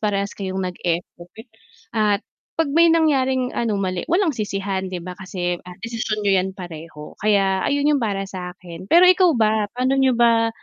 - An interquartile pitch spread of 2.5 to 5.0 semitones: No, wide, 5.4 semitones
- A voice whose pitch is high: Yes, high, 205 Hz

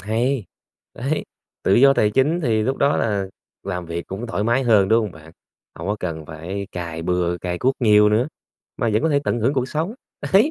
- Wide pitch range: Yes, wide, 6.5 semitones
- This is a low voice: Yes, low, 105 Hz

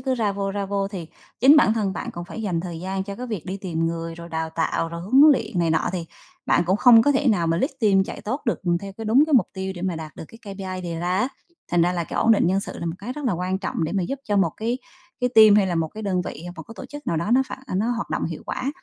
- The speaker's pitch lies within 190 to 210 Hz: Yes, high, 195 Hz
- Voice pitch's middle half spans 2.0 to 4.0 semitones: No, average, 4.6 semitones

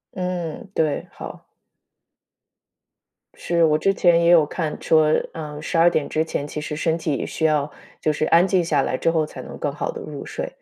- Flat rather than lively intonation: Yes, narrow, 2.3 semitones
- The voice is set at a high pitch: No, medium, 160 Hz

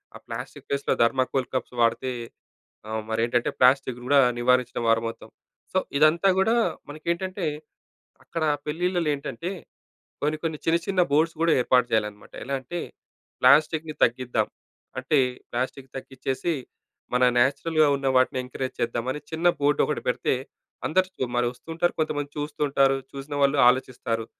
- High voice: No, medium, 140 Hz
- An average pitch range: Yes, average, 3.8 semitones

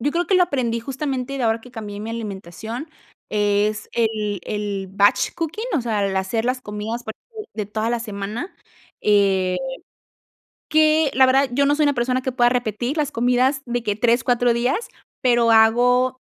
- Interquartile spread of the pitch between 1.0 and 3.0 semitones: No, average, 3.7 semitones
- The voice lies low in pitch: No, high, 235 Hz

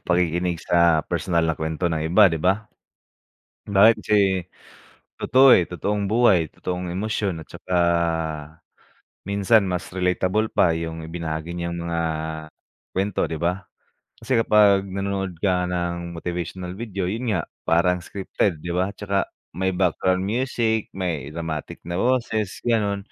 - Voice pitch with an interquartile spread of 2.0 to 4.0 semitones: Yes, average, 2.8 semitones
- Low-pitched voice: Yes, very low, 90 Hz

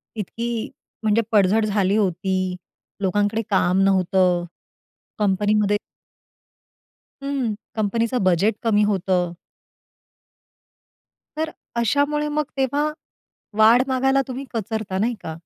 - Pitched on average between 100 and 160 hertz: No, high, 210 Hz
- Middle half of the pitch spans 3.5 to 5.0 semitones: Yes, average, 3.8 semitones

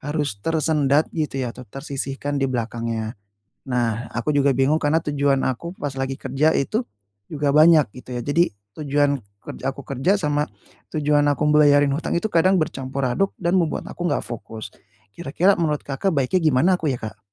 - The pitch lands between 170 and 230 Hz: No, medium, 145 Hz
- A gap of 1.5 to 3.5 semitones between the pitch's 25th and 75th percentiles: Yes, average, 3.1 semitones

